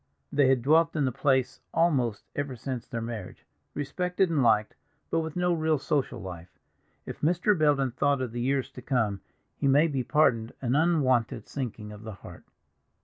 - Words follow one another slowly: No, average, 180 wpm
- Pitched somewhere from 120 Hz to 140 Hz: Yes, low, 135 Hz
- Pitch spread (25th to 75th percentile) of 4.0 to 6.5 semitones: Yes, average, 4.7 semitones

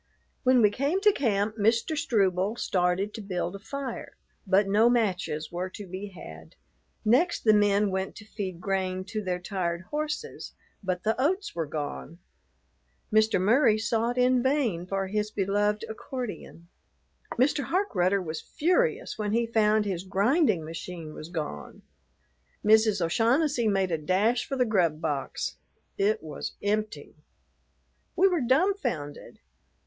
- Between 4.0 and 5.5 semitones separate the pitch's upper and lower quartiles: Yes, average, 4.7 semitones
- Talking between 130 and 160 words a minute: Yes, average, 145 wpm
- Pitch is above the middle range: Yes, high, 210 Hz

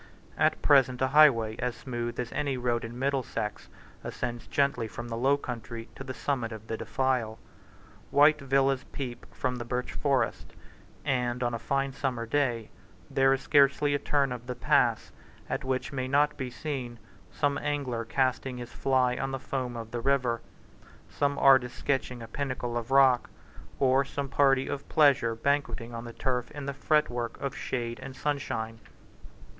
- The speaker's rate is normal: Yes, average, 170 wpm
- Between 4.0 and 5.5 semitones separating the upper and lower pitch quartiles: No, narrow, 2.5 semitones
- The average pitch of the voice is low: Yes, low, 130 Hz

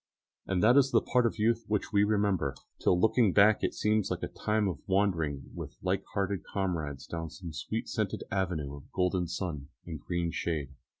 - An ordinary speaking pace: Yes, average, 195 wpm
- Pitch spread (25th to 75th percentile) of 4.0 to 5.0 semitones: Yes, average, 4.4 semitones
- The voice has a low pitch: Yes, very low, 95 Hz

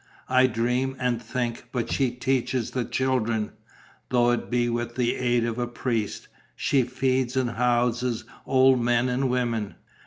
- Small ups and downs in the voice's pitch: Yes, narrow, 1.4 semitones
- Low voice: Yes, low, 125 Hz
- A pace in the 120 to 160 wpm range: Yes, average, 155 wpm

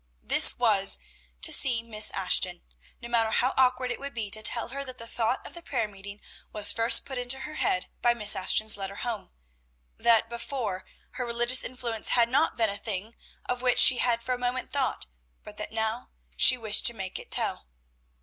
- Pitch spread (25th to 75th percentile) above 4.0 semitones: No, average, 2.9 semitones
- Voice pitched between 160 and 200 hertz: No, high, 235 Hz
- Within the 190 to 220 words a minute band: Yes, average, 200 wpm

